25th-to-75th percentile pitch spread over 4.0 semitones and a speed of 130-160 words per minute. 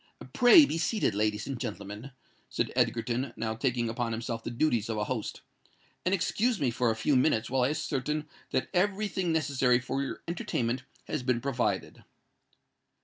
No: average, 5.0 semitones; average, 170 wpm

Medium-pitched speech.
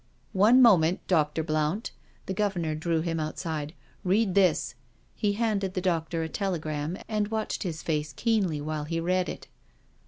Yes: medium, 170 Hz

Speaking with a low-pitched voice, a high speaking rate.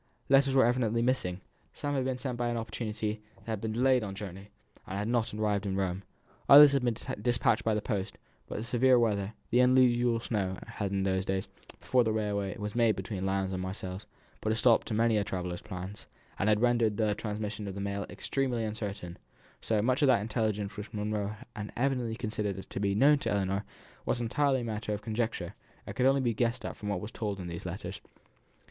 Yes: low, 110 Hz; fast, 220 wpm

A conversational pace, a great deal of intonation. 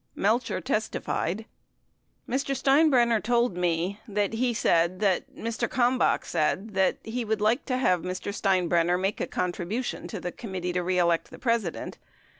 No: average, 160 wpm; average, 4.8 semitones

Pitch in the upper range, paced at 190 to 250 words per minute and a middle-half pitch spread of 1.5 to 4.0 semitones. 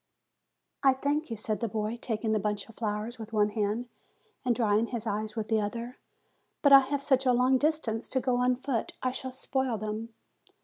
Yes: high, 230 Hz; fast, 205 wpm; average, 3.2 semitones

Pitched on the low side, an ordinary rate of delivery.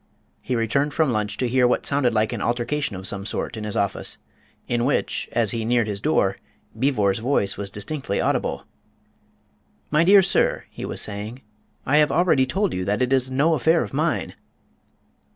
Yes: low, 125 Hz; average, 185 wpm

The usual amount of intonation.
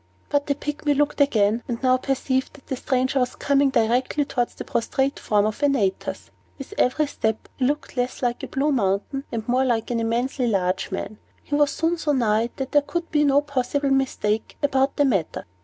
Yes: average, 3.6 semitones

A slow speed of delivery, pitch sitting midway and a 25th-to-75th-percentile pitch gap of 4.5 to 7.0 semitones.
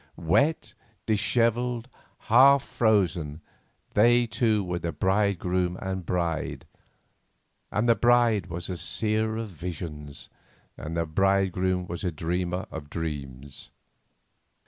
No: slow, 120 wpm; very low, 95 Hz; average, 4.8 semitones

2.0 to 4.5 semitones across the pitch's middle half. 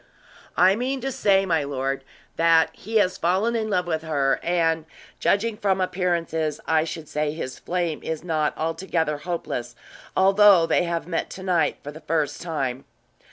Yes: average, 3.3 semitones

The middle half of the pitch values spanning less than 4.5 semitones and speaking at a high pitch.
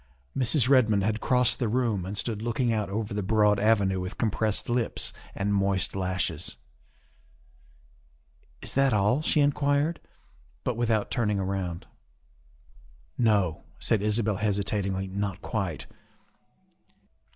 No: average, 3.5 semitones; low, 105 Hz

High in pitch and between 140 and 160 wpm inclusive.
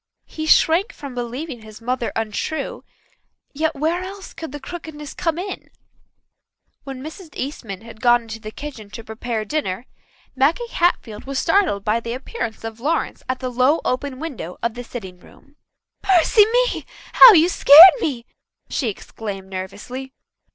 Yes: very high, 260 Hz; average, 155 wpm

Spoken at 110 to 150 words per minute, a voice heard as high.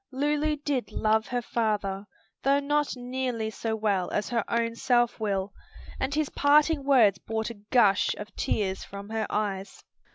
No: average, 160 wpm; high, 230 Hz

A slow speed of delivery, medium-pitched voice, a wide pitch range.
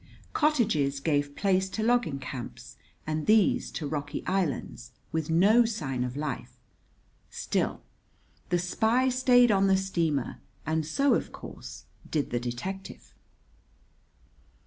Yes: slow, 125 wpm; medium, 165 Hz; wide, 7.2 semitones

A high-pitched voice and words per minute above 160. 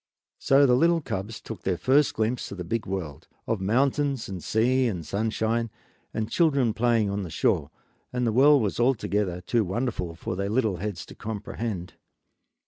No: low, 110 Hz; average, 170 wpm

